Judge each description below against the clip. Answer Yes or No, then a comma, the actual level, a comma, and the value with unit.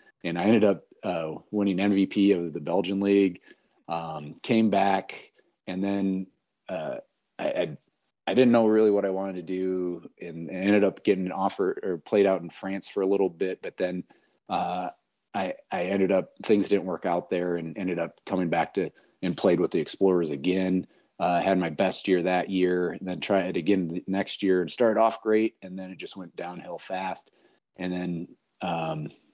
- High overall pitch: No, very low, 95 Hz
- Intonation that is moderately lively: No, narrow, 1.8 semitones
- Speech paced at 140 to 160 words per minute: No, average, 200 wpm